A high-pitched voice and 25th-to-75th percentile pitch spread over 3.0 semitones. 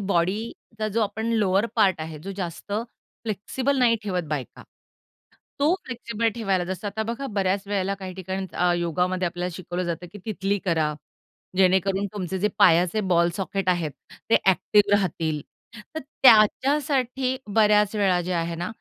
Yes: high, 195 Hz; average, 3.4 semitones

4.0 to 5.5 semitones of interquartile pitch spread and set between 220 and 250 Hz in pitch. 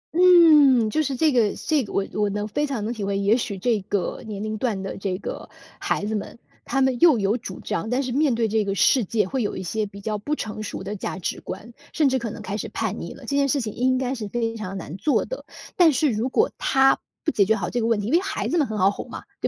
Yes: average, 4.6 semitones; high, 225 Hz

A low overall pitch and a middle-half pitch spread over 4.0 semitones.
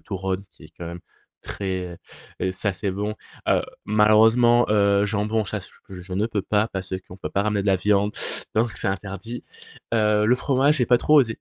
No: low, 105 Hz; narrow, 2.5 semitones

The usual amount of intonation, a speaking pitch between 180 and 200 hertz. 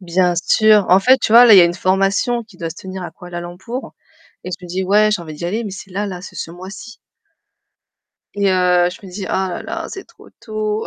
Yes: average, 3.0 semitones; high, 190 Hz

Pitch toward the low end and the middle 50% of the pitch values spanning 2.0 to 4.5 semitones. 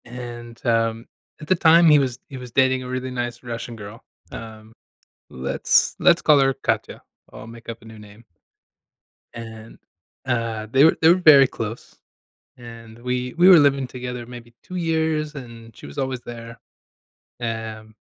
Yes: low, 120 Hz; average, 2.8 semitones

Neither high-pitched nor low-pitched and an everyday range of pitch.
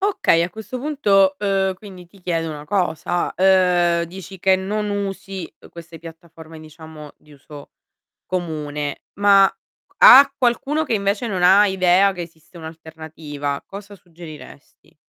Yes: medium, 180 Hz; average, 3.6 semitones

